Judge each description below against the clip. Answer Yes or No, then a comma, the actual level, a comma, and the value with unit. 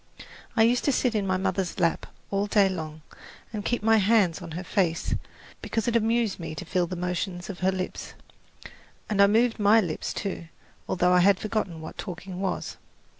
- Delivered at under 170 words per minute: No, average, 190 wpm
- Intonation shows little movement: No, average, 3.3 semitones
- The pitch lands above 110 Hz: Yes, high, 190 Hz